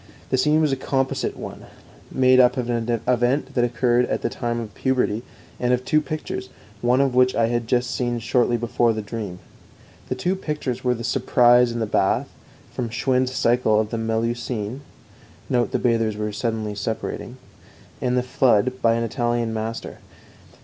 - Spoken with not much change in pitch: Yes, narrow, 1.9 semitones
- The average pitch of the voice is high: No, low, 120 Hz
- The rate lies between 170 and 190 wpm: Yes, average, 175 wpm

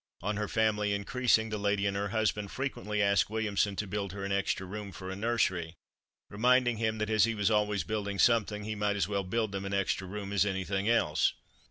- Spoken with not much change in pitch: Yes, narrow, 1.8 semitones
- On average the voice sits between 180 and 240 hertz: No, low, 105 Hz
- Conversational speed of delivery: No, fast, 215 wpm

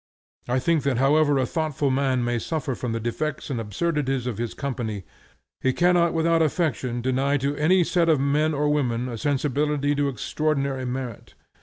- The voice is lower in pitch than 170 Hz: Yes, medium, 140 Hz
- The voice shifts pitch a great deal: No, average, 3.3 semitones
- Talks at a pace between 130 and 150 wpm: No, average, 175 wpm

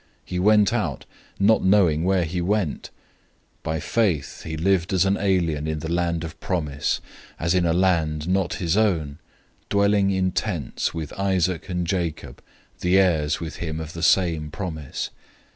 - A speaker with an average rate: Yes, average, 165 wpm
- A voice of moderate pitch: No, very low, 85 Hz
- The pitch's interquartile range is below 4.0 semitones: Yes, average, 3.3 semitones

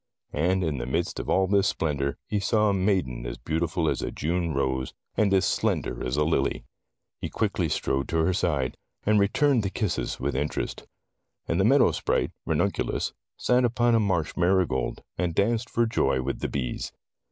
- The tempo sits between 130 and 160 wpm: No, average, 185 wpm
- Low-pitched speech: Yes, very low, 90 Hz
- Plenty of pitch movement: Yes, wide, 6.0 semitones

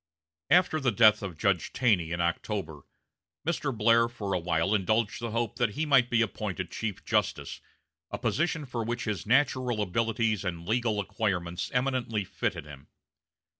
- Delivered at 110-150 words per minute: No, average, 160 wpm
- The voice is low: Yes, low, 110 Hz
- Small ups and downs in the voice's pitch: No, average, 4.1 semitones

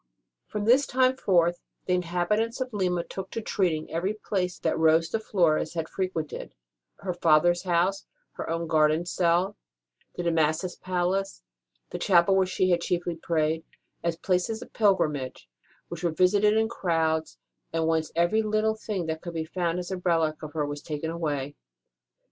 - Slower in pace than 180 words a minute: Yes, average, 170 wpm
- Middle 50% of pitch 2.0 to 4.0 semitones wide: Yes, average, 3.0 semitones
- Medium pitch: Yes, medium, 175 Hz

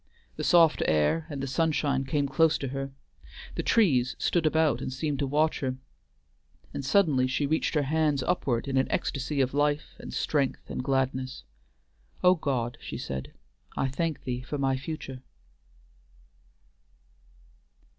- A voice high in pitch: No, medium, 140 Hz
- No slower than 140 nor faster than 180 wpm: Yes, average, 150 wpm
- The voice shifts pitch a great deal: No, average, 2.9 semitones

